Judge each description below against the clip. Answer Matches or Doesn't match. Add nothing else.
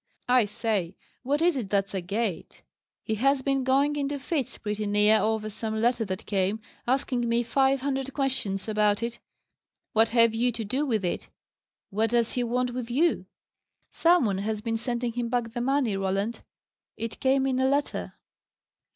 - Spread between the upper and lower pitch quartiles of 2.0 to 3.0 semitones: Doesn't match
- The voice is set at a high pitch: Matches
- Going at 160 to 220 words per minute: Matches